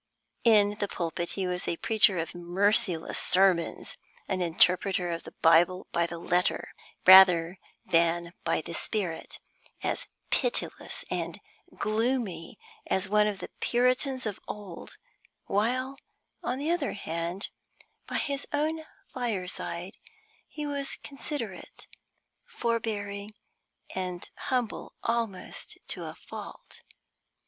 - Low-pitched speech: No, high, 200 Hz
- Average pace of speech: No, slow, 115 wpm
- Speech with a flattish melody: No, average, 5.1 semitones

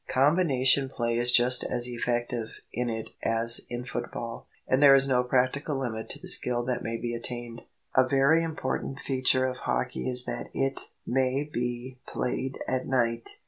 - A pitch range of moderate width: No, narrow, 1.8 semitones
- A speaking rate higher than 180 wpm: No, average, 170 wpm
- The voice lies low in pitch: Yes, low, 125 Hz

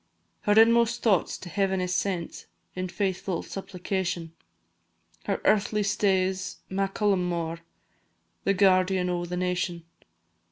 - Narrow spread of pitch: Yes, narrow, 1.8 semitones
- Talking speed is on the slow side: Yes, slow, 115 wpm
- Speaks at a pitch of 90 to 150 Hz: No, high, 190 Hz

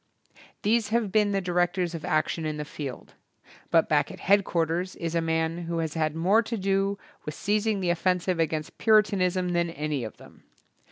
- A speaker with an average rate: Yes, average, 185 wpm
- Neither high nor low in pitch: Yes, medium, 175 Hz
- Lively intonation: No, average, 3.4 semitones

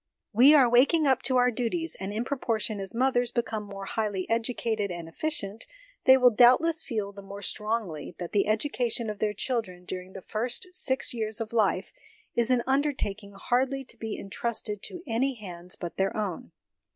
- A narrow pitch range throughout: No, average, 4.0 semitones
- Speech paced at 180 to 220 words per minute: Yes, average, 185 wpm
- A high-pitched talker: Yes, high, 225 Hz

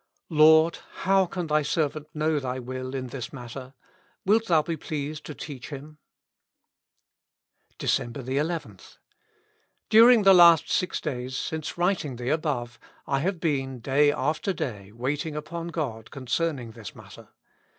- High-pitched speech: No, medium, 150 Hz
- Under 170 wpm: Yes, average, 150 wpm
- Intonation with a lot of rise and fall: No, average, 4.2 semitones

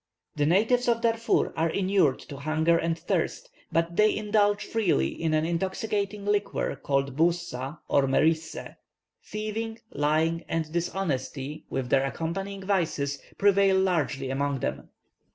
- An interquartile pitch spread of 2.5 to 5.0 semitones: No, wide, 5.5 semitones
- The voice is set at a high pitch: No, medium, 165 Hz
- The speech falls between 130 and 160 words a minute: Yes, slow, 135 wpm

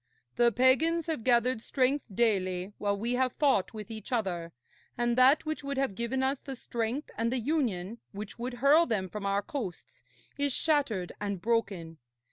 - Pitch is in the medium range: No, high, 235 Hz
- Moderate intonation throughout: Yes, average, 4.9 semitones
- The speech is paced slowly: No, average, 175 wpm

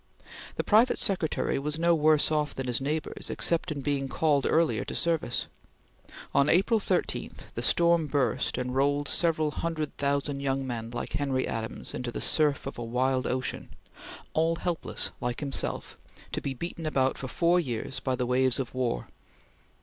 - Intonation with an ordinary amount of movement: Yes, average, 3.6 semitones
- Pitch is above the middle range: No, medium, 140 Hz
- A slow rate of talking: No, average, 170 wpm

